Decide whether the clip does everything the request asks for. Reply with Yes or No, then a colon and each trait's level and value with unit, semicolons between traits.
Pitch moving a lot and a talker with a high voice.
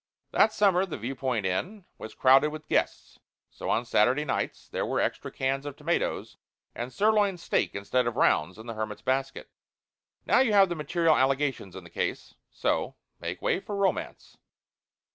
No: wide, 7.3 semitones; low, 135 Hz